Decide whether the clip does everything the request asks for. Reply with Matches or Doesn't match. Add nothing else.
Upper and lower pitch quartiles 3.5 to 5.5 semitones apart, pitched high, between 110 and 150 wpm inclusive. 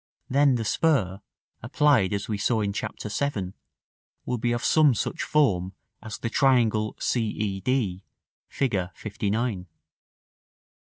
Doesn't match